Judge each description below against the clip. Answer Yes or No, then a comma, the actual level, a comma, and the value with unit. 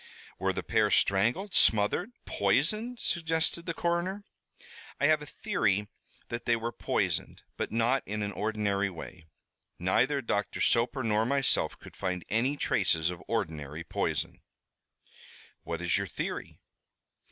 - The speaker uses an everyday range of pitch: No, wide, 7.2 semitones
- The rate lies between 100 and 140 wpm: Yes, slow, 135 wpm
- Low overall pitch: Yes, low, 115 Hz